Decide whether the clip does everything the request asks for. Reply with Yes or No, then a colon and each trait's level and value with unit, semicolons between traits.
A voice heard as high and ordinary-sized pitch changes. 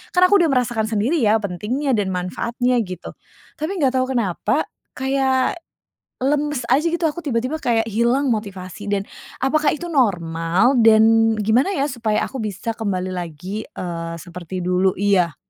No: high, 225 Hz; wide, 5.8 semitones